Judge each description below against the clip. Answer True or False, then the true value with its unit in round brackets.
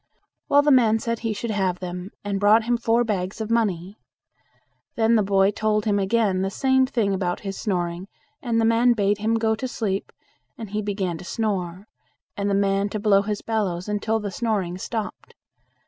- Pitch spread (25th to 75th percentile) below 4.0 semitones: True (2.6 semitones)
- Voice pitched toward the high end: True (210 Hz)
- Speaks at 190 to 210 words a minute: True (195 wpm)